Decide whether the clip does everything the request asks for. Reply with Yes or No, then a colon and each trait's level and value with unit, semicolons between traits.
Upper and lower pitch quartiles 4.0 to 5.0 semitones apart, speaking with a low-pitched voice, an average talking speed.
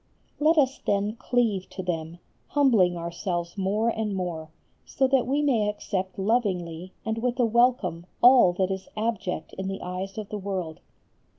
No: average, 4.6 semitones; high, 200 Hz; average, 165 wpm